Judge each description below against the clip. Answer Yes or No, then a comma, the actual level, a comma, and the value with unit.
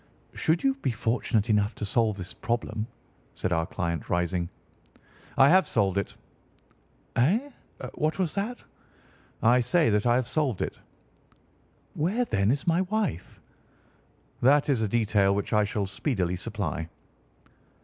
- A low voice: Yes, low, 115 Hz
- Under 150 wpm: Yes, average, 140 wpm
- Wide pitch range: Yes, wide, 7.5 semitones